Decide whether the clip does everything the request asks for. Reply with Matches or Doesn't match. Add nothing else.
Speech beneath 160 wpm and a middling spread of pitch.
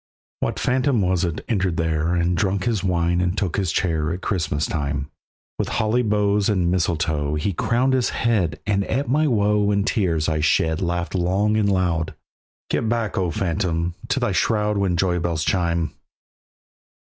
Doesn't match